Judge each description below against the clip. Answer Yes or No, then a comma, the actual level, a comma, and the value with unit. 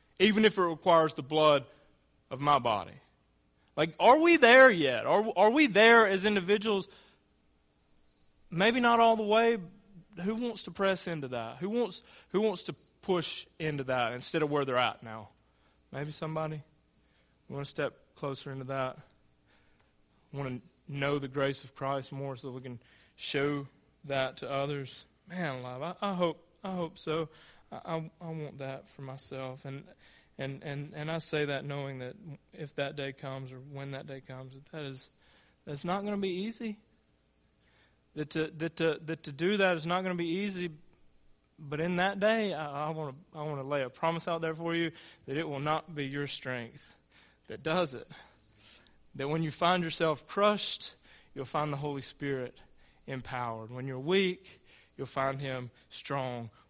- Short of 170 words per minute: No, average, 180 wpm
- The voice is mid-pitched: Yes, medium, 150 Hz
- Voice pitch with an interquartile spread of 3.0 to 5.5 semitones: Yes, average, 4.7 semitones